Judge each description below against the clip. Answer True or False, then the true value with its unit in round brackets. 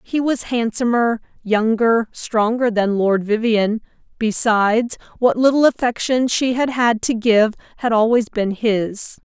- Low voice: False (230 Hz)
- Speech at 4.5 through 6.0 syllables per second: False (4.1 syllables/s)